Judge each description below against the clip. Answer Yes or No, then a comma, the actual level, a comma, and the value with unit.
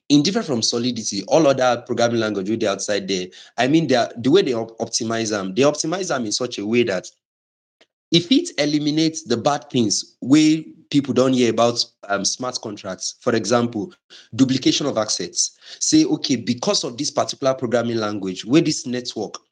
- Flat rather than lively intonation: No, average, 5.2 semitones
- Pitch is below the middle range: Yes, low, 120 Hz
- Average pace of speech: Yes, average, 180 wpm